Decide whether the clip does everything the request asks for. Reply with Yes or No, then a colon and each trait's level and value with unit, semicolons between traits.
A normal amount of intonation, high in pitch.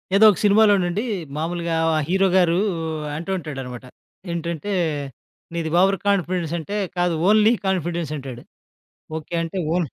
No: average, 3.2 semitones; medium, 175 Hz